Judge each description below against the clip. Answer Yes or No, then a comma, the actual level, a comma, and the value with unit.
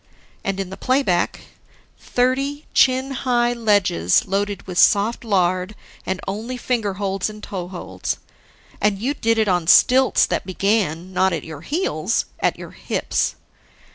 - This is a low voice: No, high, 205 Hz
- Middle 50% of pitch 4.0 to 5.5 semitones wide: Yes, average, 4.7 semitones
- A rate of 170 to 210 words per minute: No, average, 145 wpm